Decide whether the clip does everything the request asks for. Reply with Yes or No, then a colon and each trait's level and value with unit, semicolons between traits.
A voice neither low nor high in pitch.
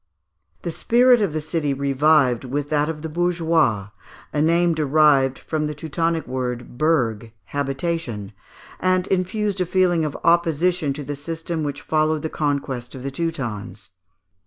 Yes: medium, 150 Hz